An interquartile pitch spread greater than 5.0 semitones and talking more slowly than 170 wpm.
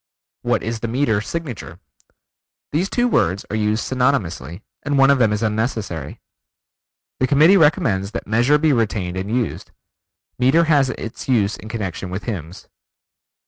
Yes: wide, 5.5 semitones; average, 150 wpm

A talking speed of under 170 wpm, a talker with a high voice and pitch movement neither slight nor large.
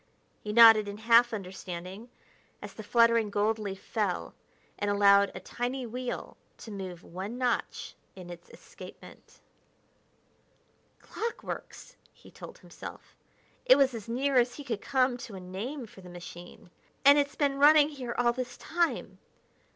Yes: average, 150 wpm; high, 230 Hz; average, 4.3 semitones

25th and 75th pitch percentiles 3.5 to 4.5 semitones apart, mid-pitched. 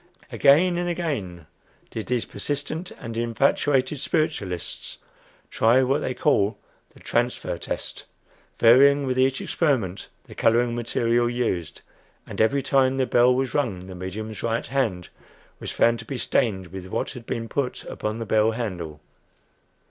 No: average, 4.1 semitones; low, 120 Hz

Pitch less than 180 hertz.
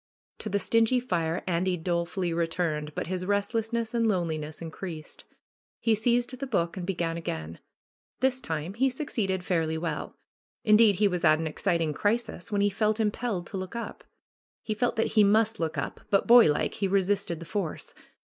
No: high, 190 Hz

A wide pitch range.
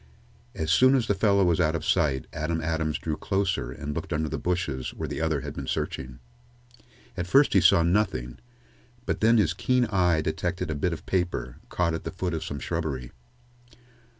No: average, 3.3 semitones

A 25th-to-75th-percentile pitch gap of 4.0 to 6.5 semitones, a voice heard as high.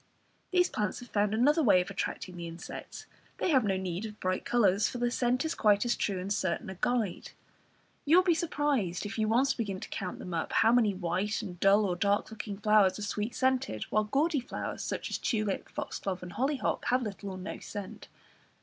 Yes: average, 4.5 semitones; high, 210 Hz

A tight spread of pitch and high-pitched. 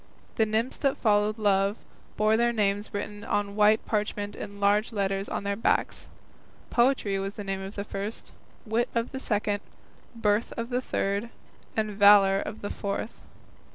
Yes: narrow, 1.7 semitones; high, 210 Hz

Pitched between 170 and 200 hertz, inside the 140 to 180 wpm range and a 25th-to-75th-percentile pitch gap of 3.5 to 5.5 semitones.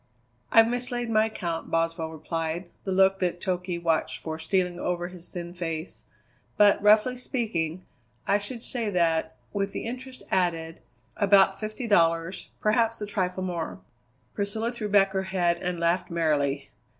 Yes: medium, 185 Hz; average, 150 wpm; average, 4.0 semitones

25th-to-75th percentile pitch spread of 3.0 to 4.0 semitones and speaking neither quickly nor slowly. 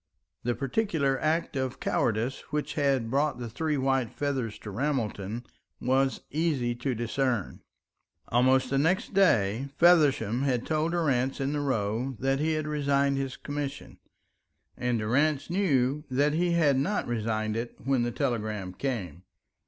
Yes: average, 3.6 semitones; average, 145 wpm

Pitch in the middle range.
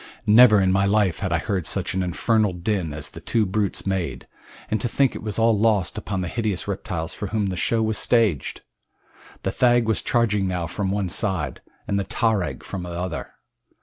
No: low, 100 Hz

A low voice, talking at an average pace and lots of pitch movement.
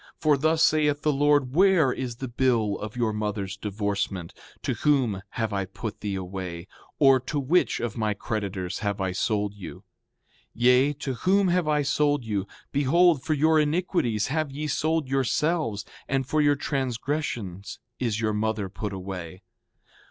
Yes: low, 125 Hz; average, 160 wpm; wide, 6.4 semitones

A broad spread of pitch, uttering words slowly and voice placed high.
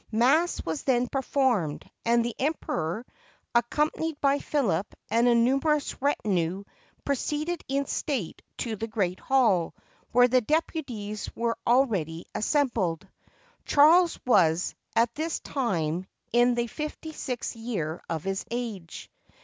Yes: wide, 6.2 semitones; slow, 125 wpm; high, 240 Hz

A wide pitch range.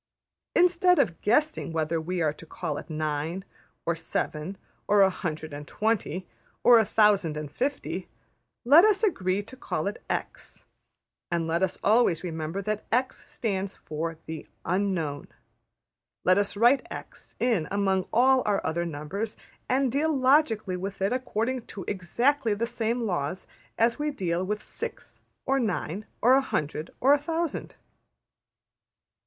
Yes: wide, 6.7 semitones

